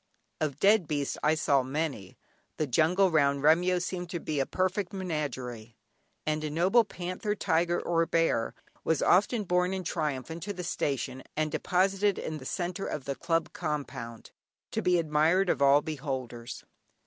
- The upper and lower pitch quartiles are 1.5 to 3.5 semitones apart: No, average, 4.3 semitones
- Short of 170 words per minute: Yes, average, 160 wpm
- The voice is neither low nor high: Yes, medium, 160 Hz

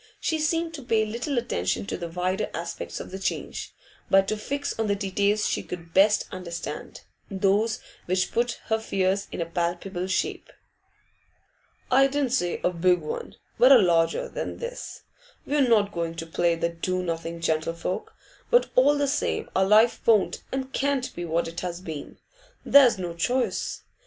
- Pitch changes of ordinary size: No, wide, 6.0 semitones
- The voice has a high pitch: Yes, high, 195 Hz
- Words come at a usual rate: Yes, average, 170 wpm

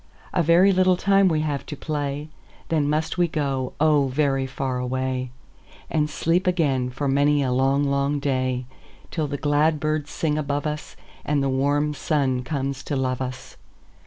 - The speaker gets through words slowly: No, average, 155 wpm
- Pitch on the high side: No, medium, 145 Hz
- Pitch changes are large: No, narrow, 2.6 semitones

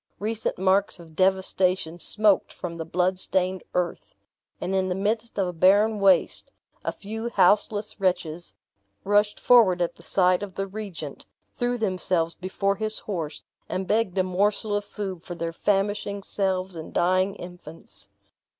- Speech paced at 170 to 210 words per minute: No, average, 155 wpm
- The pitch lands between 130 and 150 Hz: No, high, 190 Hz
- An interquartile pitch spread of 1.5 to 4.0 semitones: Yes, narrow, 2.4 semitones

